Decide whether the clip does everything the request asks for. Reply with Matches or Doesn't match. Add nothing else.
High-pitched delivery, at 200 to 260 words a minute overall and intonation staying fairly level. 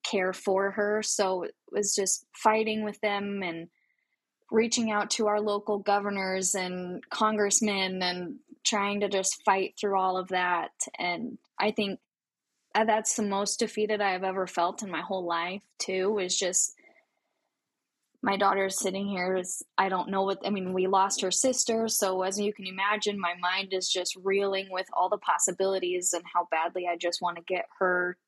Doesn't match